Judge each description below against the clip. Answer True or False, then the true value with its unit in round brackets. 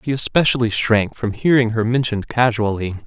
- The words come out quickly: False (155 wpm)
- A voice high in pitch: False (115 Hz)